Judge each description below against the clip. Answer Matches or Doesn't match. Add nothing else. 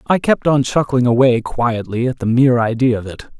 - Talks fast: Matches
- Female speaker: Doesn't match